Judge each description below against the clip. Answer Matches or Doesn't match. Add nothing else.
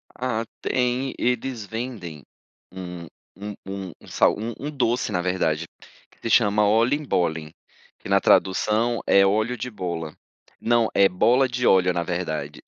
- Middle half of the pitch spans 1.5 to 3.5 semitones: Doesn't match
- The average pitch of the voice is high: Doesn't match